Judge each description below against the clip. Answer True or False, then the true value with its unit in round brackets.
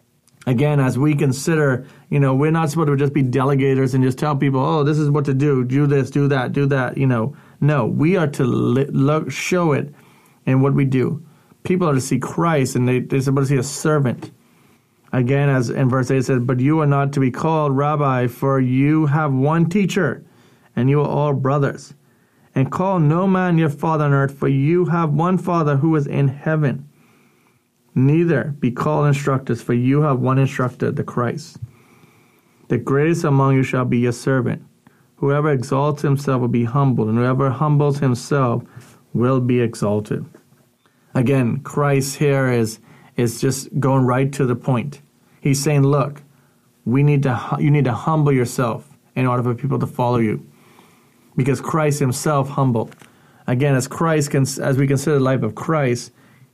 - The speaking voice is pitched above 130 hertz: True (140 Hz)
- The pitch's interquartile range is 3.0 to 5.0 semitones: False (2.6 semitones)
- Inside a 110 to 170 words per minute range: False (185 wpm)